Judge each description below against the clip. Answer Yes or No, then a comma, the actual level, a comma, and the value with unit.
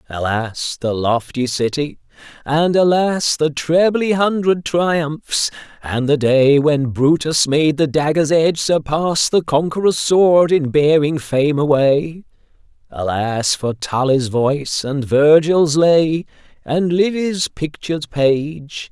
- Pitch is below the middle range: No, medium, 150 Hz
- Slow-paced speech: Yes, slow, 120 wpm